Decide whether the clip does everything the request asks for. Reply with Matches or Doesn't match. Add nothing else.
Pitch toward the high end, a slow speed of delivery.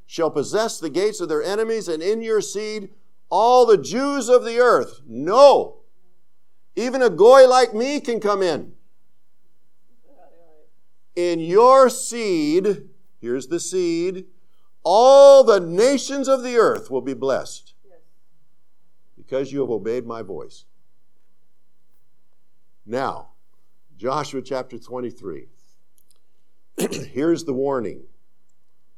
Matches